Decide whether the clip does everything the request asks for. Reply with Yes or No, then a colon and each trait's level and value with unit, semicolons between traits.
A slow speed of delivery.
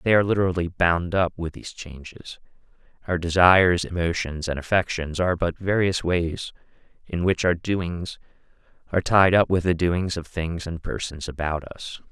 No: average, 165 wpm